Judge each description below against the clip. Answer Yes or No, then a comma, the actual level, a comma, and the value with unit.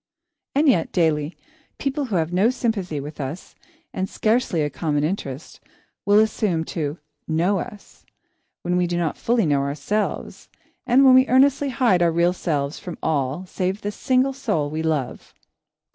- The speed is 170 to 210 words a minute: No, average, 160 wpm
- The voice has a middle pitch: Yes, medium, 180 Hz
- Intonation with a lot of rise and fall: Yes, wide, 6.3 semitones